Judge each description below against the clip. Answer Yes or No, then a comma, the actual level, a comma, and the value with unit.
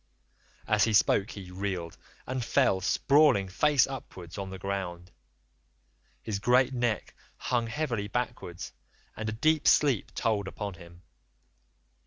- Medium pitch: No, low, 105 Hz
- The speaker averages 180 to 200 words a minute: No, slow, 135 wpm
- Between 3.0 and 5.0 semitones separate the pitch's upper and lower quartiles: Yes, average, 4.7 semitones